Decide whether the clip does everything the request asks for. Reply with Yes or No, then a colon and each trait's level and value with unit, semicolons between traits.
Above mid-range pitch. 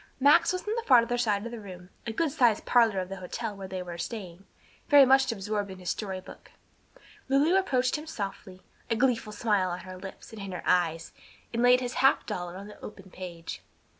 Yes: high, 210 Hz